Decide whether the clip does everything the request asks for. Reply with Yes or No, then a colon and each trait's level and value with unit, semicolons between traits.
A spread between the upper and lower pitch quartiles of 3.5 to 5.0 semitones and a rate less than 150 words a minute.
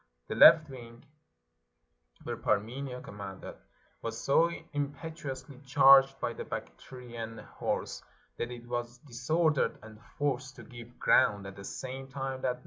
No: average, 2.7 semitones; average, 140 wpm